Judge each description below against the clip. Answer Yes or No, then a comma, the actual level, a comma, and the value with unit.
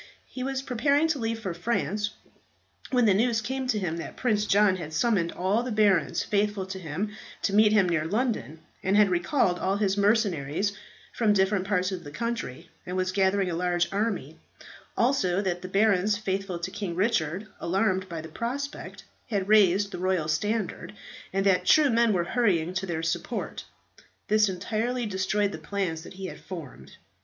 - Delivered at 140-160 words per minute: No, average, 180 wpm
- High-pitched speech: Yes, high, 195 Hz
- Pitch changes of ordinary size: Yes, average, 3.2 semitones